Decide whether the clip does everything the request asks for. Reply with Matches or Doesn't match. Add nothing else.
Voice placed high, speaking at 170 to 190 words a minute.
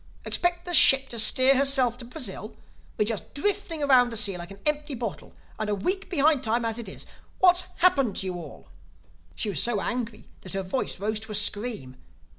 Doesn't match